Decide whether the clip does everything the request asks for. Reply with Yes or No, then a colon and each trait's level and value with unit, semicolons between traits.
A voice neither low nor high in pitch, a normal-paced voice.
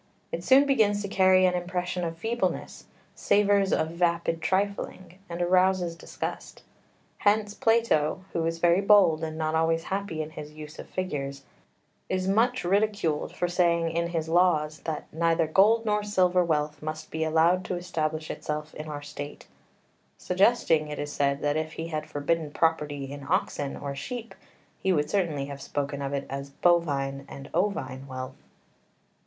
Yes: medium, 165 Hz; average, 165 wpm